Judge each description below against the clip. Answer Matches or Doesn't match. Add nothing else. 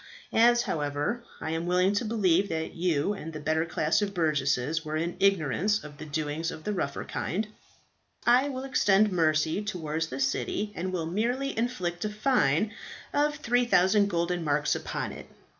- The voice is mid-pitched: Matches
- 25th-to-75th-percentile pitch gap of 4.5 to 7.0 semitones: Matches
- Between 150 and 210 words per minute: Matches